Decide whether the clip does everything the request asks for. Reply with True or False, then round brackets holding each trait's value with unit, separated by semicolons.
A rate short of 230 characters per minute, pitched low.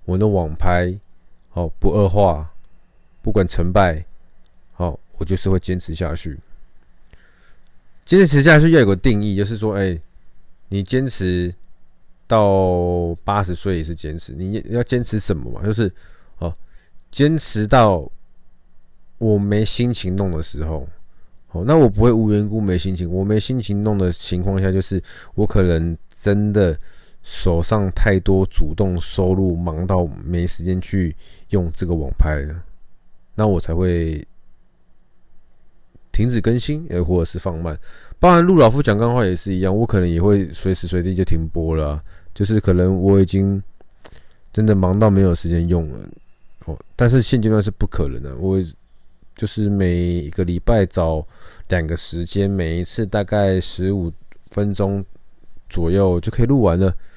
True (220 characters per minute; 95 Hz)